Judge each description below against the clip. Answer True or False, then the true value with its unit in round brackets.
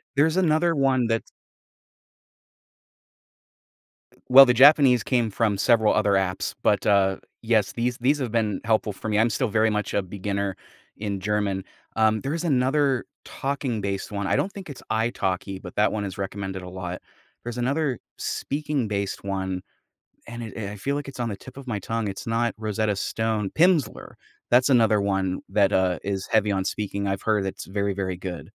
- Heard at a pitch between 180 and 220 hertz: False (110 Hz)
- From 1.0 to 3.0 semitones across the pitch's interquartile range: False (4.2 semitones)